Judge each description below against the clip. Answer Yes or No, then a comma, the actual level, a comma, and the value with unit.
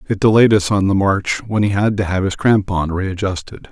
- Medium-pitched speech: No, low, 100 Hz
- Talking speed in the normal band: No, fast, 225 wpm